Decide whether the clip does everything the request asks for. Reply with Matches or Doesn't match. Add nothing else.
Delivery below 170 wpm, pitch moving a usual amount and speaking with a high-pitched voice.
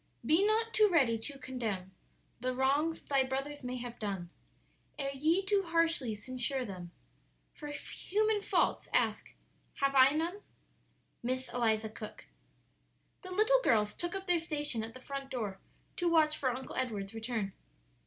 Doesn't match